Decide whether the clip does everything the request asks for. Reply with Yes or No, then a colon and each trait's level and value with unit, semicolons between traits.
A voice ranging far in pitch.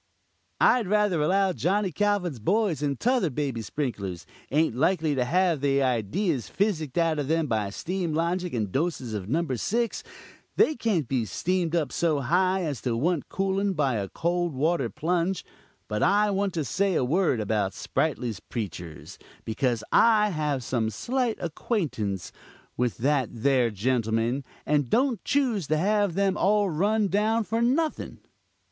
Yes: wide, 7.7 semitones